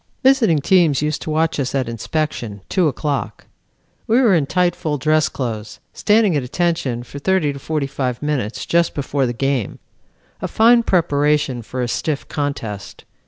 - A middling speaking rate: Yes, average, 165 wpm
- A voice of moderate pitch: Yes, medium, 145 Hz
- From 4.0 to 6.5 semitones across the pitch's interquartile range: Yes, average, 4.6 semitones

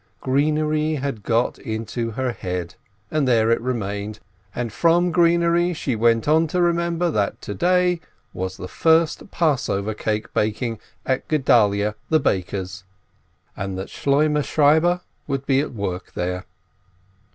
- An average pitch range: No, wide, 7.0 semitones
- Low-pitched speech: Yes, low, 130 Hz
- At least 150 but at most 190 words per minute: No, average, 140 wpm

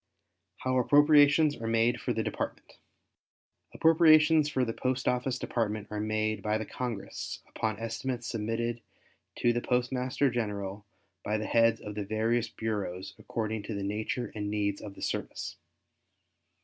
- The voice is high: No, low, 115 Hz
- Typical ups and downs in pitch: Yes, average, 3.0 semitones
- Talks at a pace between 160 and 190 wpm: No, average, 150 wpm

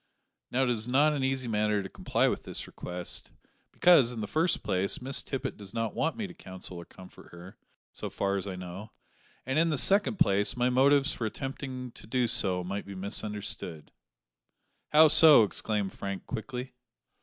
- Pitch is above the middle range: No, low, 115 Hz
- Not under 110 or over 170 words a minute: No, average, 185 wpm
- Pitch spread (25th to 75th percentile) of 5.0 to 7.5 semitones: Yes, average, 5.3 semitones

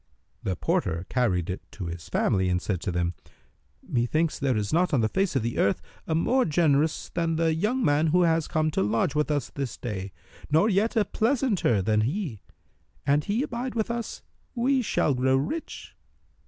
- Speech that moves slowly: No, average, 190 wpm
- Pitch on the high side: No, medium, 150 Hz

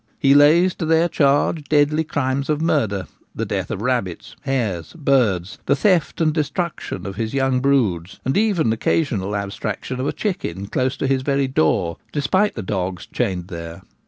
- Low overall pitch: Yes, low, 130 Hz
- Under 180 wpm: Yes, average, 165 wpm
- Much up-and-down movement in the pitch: Yes, wide, 7.3 semitones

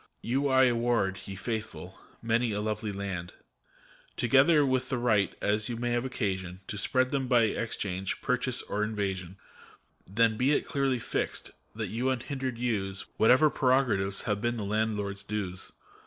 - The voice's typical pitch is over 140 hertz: No, low, 115 Hz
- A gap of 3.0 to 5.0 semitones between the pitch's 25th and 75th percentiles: Yes, average, 4.1 semitones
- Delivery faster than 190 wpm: No, average, 160 wpm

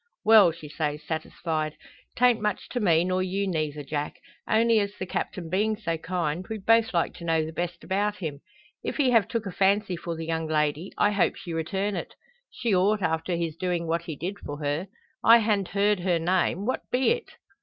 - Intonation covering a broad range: No, average, 4.2 semitones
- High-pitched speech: No, medium, 180 Hz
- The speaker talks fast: Yes, fast, 210 wpm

